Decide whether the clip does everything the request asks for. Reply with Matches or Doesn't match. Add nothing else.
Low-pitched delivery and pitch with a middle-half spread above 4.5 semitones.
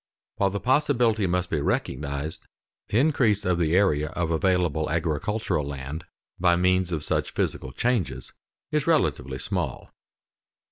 Matches